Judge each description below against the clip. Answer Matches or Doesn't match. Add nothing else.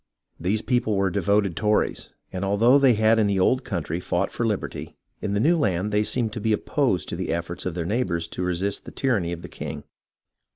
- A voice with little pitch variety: Doesn't match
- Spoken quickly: Matches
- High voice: Doesn't match